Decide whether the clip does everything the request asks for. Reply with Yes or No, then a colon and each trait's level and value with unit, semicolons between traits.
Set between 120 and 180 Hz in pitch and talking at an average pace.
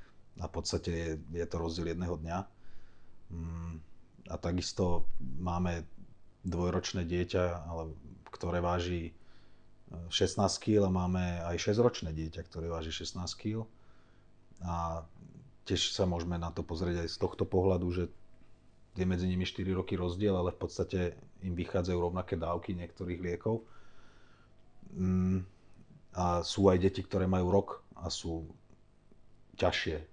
No: very low, 90 Hz; average, 125 wpm